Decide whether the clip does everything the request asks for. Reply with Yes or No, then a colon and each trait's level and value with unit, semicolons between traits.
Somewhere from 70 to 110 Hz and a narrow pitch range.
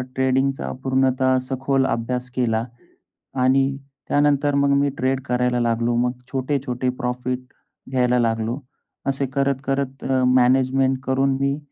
No: low, 130 Hz; narrow, 1.6 semitones